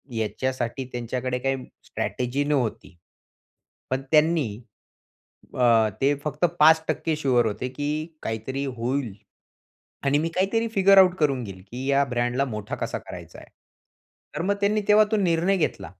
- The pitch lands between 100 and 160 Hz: Yes, medium, 140 Hz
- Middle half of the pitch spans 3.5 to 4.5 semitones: No, average, 4.9 semitones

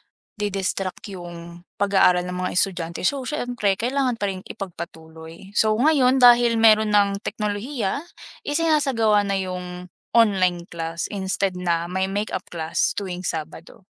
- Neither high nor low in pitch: No, high, 195 Hz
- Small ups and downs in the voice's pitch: No, average, 4.2 semitones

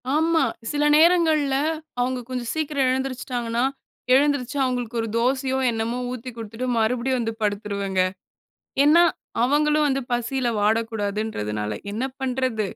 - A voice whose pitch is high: Yes, very high, 250 Hz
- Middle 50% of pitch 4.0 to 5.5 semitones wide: No, average, 3.4 semitones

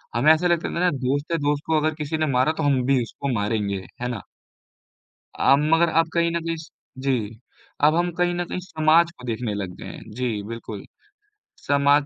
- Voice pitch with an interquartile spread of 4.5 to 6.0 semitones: Yes, average, 5.0 semitones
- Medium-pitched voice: Yes, medium, 145 Hz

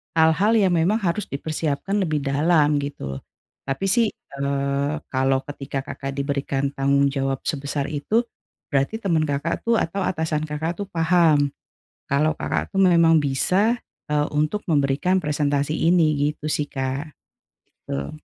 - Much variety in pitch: No, average, 3.2 semitones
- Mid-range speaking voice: Yes, medium, 150 Hz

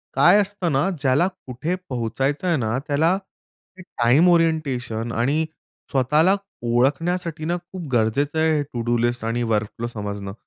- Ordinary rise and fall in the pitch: No, wide, 6.0 semitones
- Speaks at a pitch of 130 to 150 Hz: Yes, medium, 140 Hz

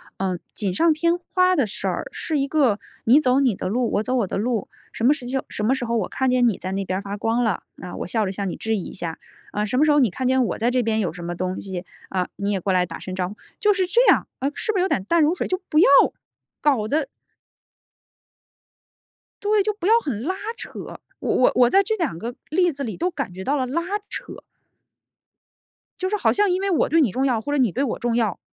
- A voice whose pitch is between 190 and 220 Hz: No, very high, 250 Hz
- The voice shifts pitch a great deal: Yes, wide, 7.6 semitones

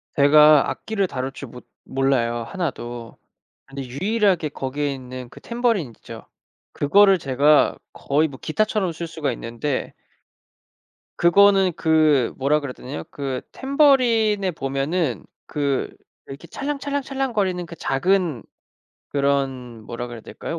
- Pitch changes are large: Yes, wide, 6.4 semitones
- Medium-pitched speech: Yes, medium, 150 Hz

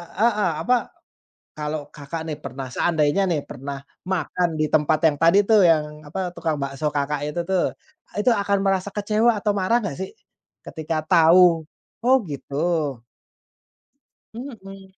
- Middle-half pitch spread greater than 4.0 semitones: Yes, average, 4.7 semitones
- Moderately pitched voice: Yes, medium, 165 Hz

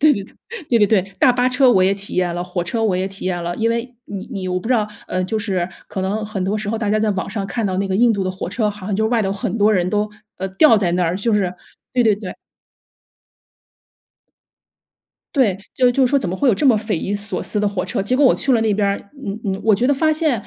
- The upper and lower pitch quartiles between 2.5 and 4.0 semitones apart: Yes, average, 3.3 semitones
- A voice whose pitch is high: Yes, high, 205 Hz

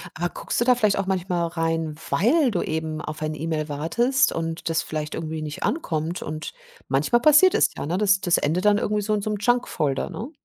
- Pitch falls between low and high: Yes, medium, 170 Hz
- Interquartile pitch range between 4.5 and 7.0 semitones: Yes, average, 5.2 semitones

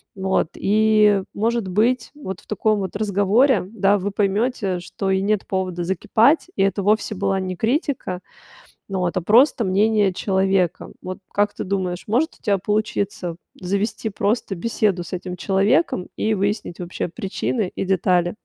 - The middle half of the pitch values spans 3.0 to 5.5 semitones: No, narrow, 2.6 semitones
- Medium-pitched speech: No, high, 200 Hz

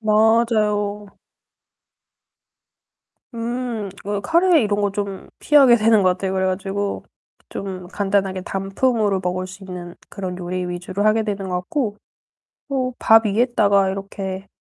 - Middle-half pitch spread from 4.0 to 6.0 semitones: No, average, 2.7 semitones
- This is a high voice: Yes, high, 200 Hz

